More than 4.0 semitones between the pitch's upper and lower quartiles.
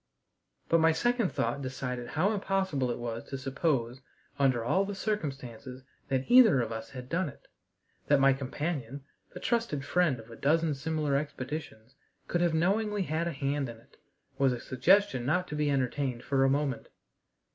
Yes: average, 4.7 semitones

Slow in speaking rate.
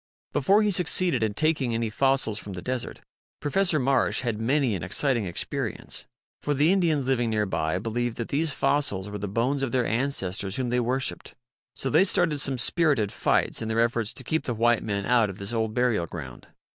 No: fast, 205 wpm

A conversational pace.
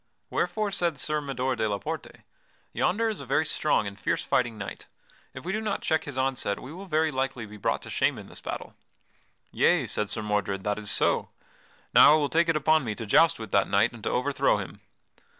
No: fast, 220 wpm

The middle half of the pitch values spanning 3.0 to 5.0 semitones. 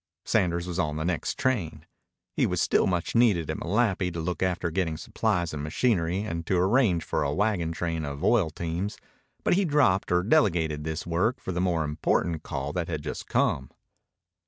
Yes: average, 3.4 semitones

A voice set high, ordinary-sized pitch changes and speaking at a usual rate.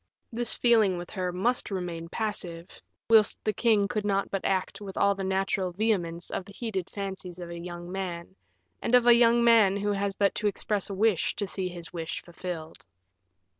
Yes: high, 195 Hz; average, 3.0 semitones; average, 195 wpm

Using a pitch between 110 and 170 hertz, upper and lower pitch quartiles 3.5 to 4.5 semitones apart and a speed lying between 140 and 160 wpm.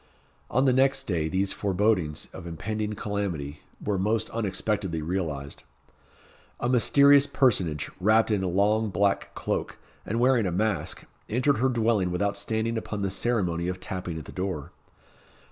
No: low, 100 Hz; average, 3.9 semitones; average, 150 wpm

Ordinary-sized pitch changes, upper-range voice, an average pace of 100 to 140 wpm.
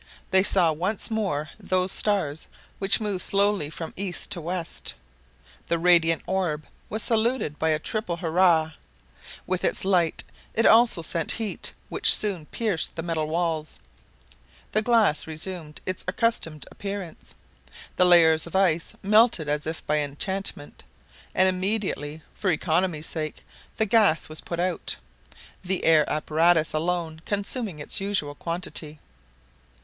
No: average, 3.8 semitones; medium, 175 Hz; slow, 135 wpm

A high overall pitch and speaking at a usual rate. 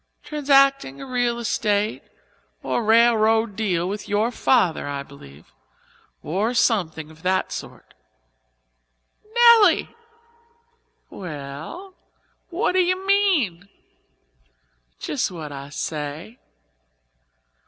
No: high, 215 Hz; slow, 90 wpm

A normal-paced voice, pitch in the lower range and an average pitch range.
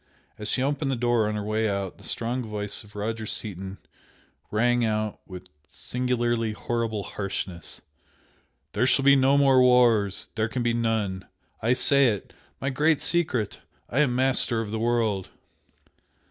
Yes: average, 160 wpm; low, 115 Hz; average, 3.2 semitones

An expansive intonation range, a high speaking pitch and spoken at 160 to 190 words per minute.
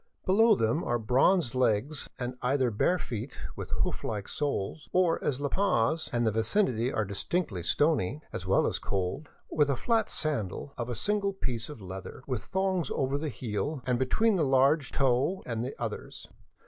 No: wide, 5.7 semitones; low, 130 Hz; average, 175 wpm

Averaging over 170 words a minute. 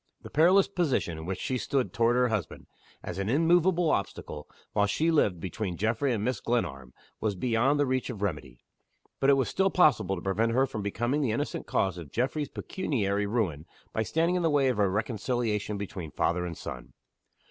Yes: average, 195 wpm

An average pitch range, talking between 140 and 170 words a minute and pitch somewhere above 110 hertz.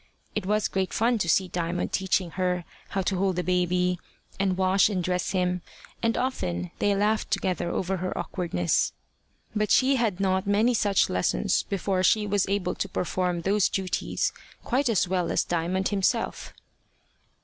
No: narrow, 2.1 semitones; average, 165 wpm; high, 190 Hz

